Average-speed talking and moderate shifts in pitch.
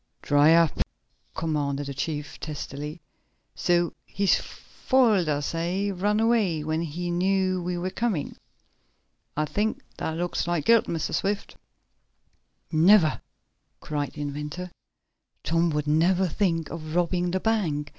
No: slow, 130 wpm; average, 3.7 semitones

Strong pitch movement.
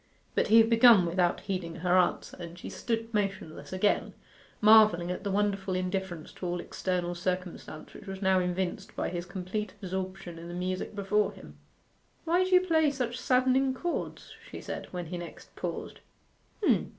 No: average, 3.5 semitones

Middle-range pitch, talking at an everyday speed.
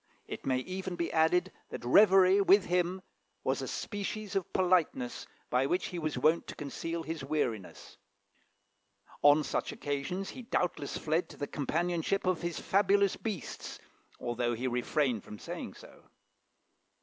Yes: medium, 165 Hz; average, 150 wpm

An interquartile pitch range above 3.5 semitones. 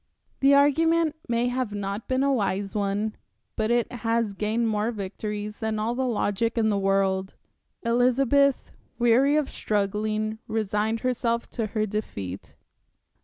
No: average, 2.9 semitones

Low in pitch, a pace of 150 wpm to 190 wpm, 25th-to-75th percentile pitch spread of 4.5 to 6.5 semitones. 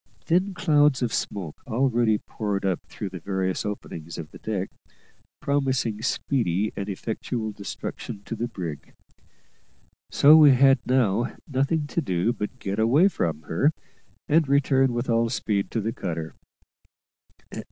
No: low, 115 Hz; average, 140 wpm; wide, 5.5 semitones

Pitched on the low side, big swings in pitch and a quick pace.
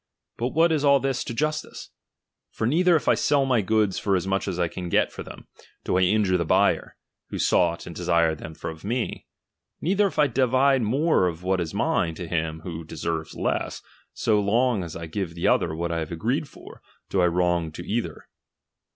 Yes: very low, 95 Hz; wide, 7.2 semitones; fast, 210 wpm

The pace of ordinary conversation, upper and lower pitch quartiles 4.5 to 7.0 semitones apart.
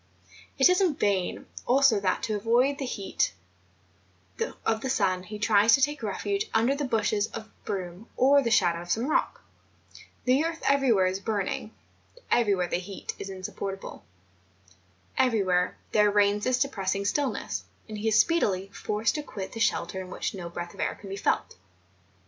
Yes: average, 170 wpm; average, 4.9 semitones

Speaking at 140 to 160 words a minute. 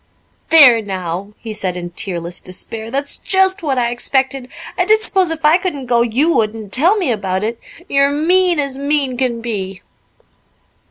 No: average, 175 wpm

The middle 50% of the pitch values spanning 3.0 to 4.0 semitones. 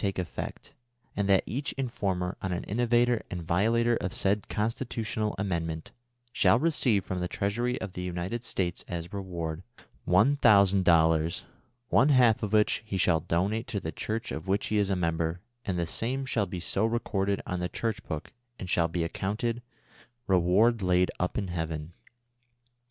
No: average, 4.4 semitones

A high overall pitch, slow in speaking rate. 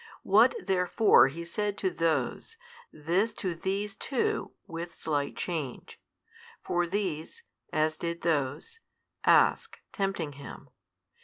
No: medium, 170 Hz; slow, 110 wpm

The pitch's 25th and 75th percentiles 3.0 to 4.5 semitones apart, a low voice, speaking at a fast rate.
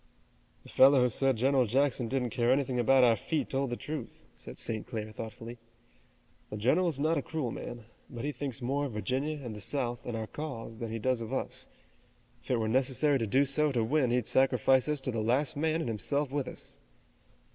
Yes: average, 3.4 semitones; low, 130 Hz; fast, 215 wpm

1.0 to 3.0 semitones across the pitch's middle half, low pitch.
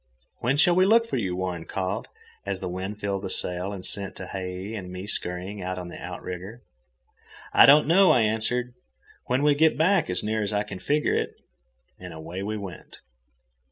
No: average, 5.2 semitones; low, 100 Hz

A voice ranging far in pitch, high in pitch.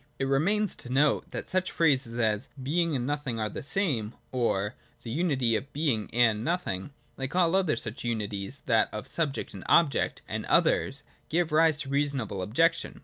No: wide, 6.1 semitones; low, 135 Hz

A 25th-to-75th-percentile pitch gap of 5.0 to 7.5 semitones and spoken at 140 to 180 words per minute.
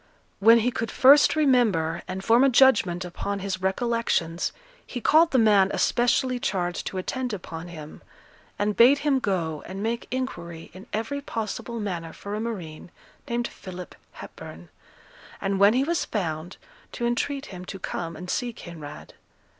Yes: wide, 5.5 semitones; average, 160 wpm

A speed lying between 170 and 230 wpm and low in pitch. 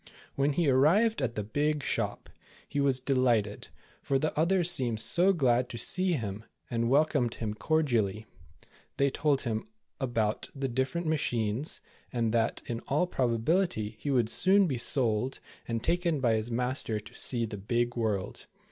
No: average, 160 wpm; low, 125 Hz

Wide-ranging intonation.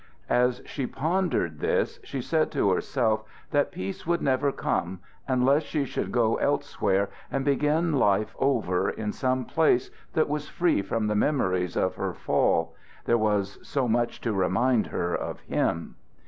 Yes: wide, 6.0 semitones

